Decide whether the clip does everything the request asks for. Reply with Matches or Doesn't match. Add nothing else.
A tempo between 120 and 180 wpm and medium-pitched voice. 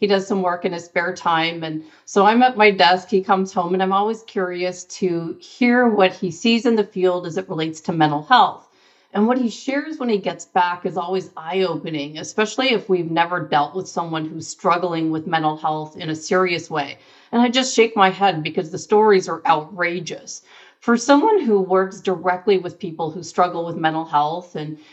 Doesn't match